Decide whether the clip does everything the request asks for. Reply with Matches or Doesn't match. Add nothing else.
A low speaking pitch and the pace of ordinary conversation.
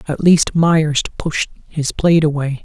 Doesn't match